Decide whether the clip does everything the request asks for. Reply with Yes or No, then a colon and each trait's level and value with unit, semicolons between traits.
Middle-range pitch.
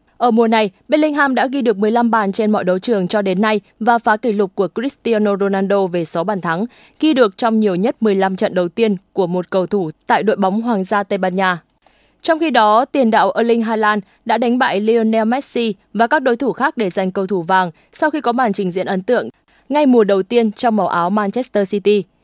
No: high, 215 Hz